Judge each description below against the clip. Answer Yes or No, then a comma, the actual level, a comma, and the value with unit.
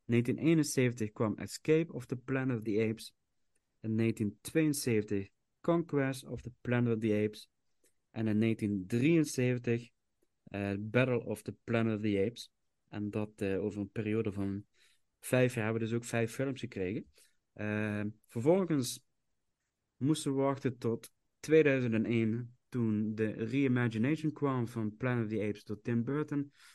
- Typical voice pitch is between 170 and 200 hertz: No, low, 115 Hz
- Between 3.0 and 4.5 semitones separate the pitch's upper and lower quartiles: Yes, average, 3.5 semitones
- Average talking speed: Yes, average, 145 wpm